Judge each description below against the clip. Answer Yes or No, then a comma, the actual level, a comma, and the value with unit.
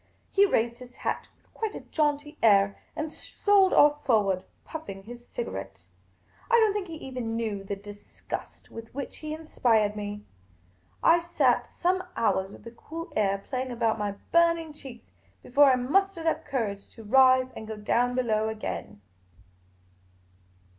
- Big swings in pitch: Yes, wide, 6.7 semitones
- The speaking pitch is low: No, high, 245 Hz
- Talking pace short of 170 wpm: Yes, average, 160 wpm